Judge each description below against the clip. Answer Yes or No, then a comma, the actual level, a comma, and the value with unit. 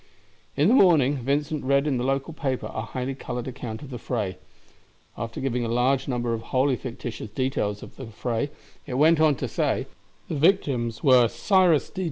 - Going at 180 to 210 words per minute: Yes, average, 190 wpm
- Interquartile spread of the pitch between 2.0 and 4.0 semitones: Yes, average, 3.4 semitones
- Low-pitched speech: Yes, low, 130 Hz